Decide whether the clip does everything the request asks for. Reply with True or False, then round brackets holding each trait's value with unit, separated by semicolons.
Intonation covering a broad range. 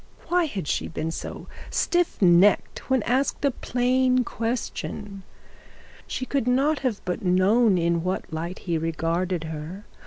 True (6.8 semitones)